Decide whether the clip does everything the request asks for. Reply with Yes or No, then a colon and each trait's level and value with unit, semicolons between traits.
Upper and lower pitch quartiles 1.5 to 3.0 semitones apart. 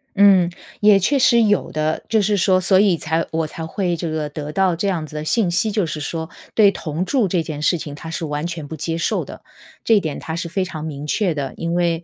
No: average, 3.7 semitones